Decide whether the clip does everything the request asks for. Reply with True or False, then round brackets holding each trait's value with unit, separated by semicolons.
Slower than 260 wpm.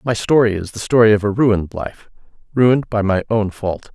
True (200 wpm)